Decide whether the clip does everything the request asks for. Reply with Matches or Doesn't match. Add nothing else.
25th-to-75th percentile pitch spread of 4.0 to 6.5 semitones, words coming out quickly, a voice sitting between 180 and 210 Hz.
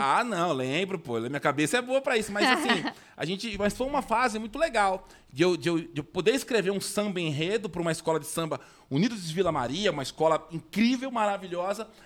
Matches